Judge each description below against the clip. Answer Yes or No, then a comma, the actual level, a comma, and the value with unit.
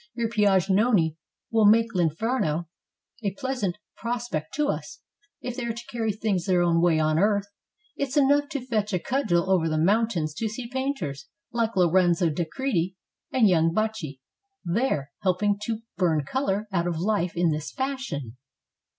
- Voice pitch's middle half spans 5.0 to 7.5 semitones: Yes, wide, 5.6 semitones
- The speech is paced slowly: No, average, 165 wpm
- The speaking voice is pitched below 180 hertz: No, high, 200 Hz